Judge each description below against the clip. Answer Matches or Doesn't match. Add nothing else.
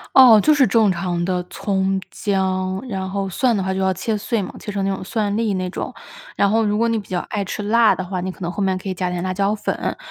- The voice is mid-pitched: Doesn't match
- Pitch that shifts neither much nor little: Doesn't match